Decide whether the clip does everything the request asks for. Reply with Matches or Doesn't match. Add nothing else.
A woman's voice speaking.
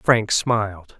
Doesn't match